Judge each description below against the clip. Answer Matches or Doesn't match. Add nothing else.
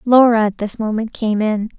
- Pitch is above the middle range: Matches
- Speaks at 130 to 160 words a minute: Doesn't match